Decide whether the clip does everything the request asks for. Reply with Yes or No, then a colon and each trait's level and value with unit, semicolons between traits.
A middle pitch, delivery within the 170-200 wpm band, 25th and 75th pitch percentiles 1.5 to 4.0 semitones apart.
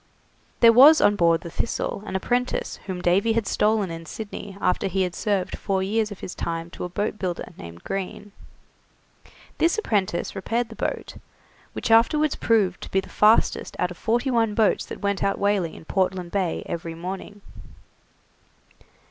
No: high, 195 Hz; average, 175 wpm; average, 3.7 semitones